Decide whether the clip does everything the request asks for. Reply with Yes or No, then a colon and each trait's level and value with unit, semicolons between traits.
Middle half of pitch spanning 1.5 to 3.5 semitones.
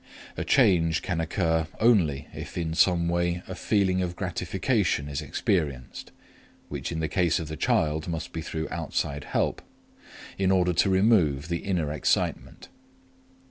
Yes: average, 2.8 semitones